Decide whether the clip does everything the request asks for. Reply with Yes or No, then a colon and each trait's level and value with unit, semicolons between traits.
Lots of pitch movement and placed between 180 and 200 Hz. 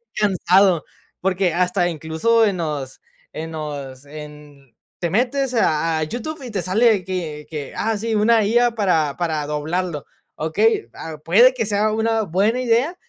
Yes: wide, 6.3 semitones; medium, 185 Hz